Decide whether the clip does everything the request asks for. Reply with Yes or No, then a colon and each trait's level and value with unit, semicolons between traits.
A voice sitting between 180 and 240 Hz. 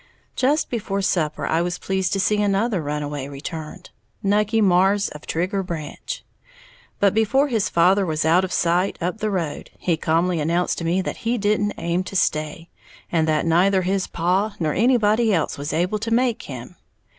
Yes: medium, 185 Hz